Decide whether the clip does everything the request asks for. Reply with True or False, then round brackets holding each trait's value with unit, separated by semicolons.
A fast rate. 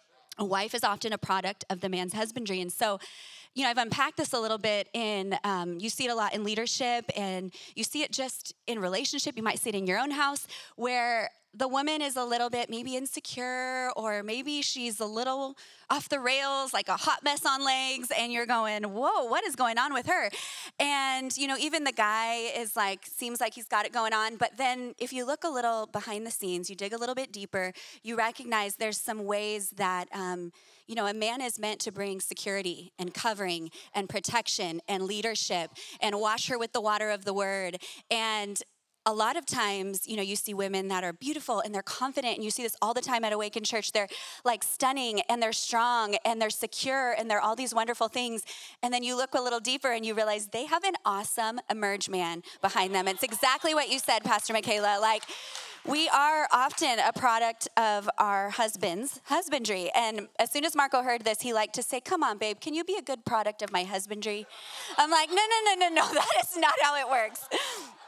True (220 wpm)